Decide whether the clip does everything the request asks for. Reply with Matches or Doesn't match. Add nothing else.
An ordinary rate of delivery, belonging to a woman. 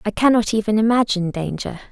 Matches